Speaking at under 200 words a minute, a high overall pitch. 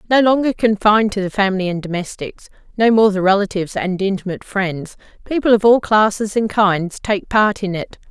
Yes: average, 170 wpm; high, 205 Hz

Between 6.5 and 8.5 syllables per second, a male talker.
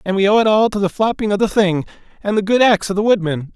Yes: 6.8 syllables/s; male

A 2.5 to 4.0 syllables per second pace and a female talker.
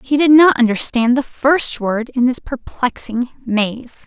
Yes: 3.8 syllables/s; female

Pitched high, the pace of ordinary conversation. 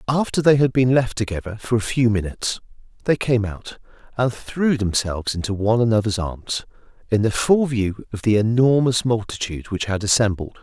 No: low, 115 Hz; average, 175 wpm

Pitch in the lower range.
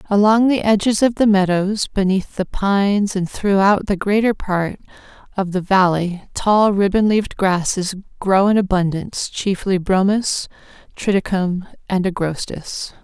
No: high, 195 Hz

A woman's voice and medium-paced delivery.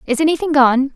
Yes: female; average, 190 wpm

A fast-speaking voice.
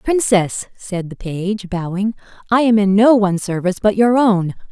No: average, 180 wpm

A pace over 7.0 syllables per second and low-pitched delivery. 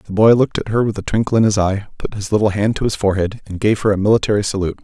Yes: 7.3 syllables/s; low, 105 Hz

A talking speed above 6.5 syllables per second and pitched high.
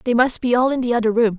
Yes: 7.1 syllables/s; high, 235 Hz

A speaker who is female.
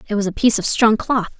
Yes: female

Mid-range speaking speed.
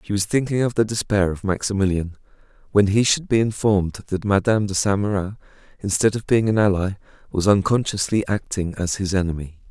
Yes: average, 180 wpm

